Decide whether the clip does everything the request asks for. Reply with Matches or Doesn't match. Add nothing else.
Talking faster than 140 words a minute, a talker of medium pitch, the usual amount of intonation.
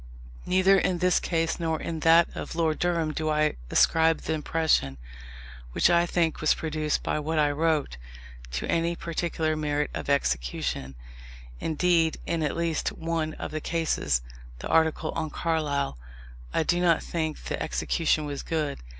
Doesn't match